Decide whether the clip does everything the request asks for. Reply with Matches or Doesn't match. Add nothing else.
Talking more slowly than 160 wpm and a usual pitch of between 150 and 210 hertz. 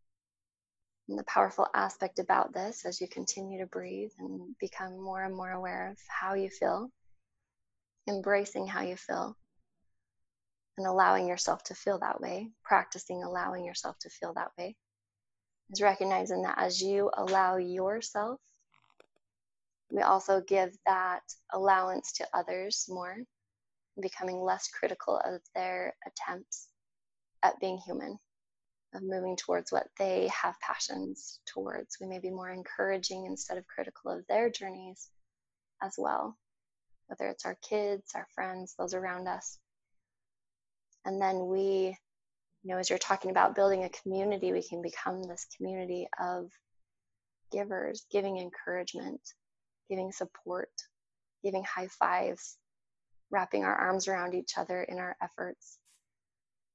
Matches